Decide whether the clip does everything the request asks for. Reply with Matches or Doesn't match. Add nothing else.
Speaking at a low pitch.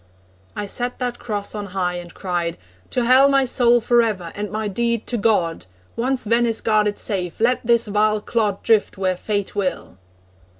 Doesn't match